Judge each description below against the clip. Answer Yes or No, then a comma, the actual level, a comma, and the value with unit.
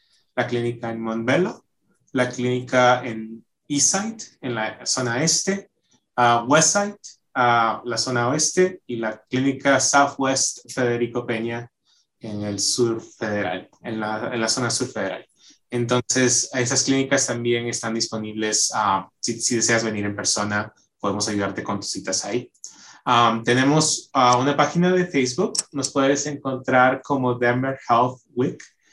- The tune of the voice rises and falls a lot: No, average, 3.0 semitones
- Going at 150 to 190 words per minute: No, average, 140 wpm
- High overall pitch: No, low, 125 Hz